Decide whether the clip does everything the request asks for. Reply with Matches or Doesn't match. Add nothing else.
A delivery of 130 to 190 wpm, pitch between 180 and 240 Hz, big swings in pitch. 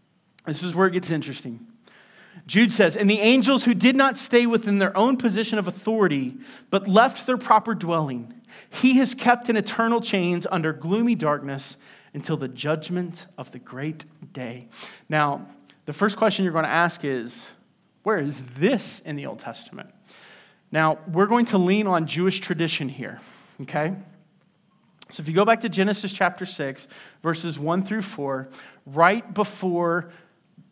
Matches